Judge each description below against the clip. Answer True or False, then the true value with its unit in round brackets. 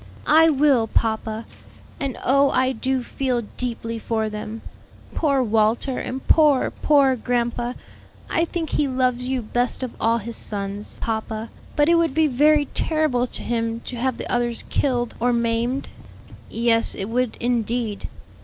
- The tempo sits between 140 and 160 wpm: True (155 wpm)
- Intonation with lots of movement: False (2.8 semitones)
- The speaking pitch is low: False (245 Hz)